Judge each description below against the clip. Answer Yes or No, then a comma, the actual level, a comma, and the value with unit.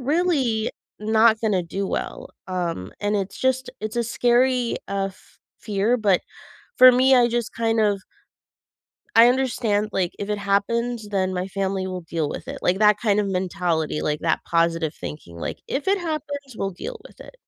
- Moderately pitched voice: No, high, 210 Hz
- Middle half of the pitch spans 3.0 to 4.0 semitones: No, average, 4.5 semitones